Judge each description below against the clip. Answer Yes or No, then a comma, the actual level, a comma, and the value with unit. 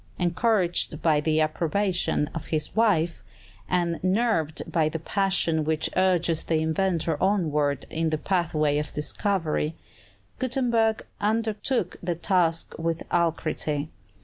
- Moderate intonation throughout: Yes, average, 3.6 semitones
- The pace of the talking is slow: Yes, slow, 120 wpm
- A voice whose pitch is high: No, medium, 170 Hz